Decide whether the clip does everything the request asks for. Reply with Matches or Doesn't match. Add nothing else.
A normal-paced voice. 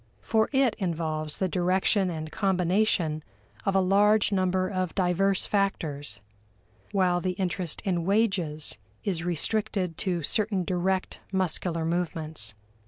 Doesn't match